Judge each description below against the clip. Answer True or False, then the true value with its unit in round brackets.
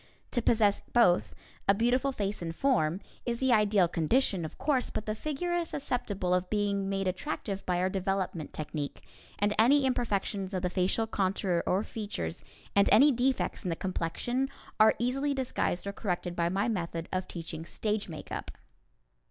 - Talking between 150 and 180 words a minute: True (170 wpm)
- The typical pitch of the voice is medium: False (200 Hz)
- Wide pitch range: False (4.9 semitones)